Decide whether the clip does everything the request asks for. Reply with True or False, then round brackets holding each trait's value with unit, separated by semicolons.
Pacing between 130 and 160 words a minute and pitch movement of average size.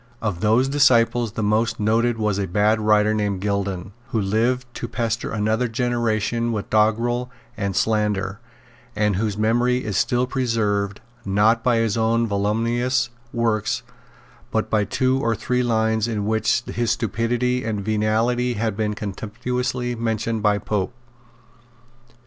False (140 wpm; 2.2 semitones)